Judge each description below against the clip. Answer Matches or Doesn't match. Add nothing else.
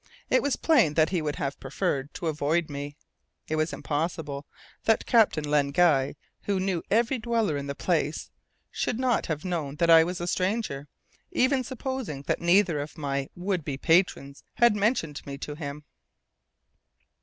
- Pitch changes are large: Matches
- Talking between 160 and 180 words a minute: Matches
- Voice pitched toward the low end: Doesn't match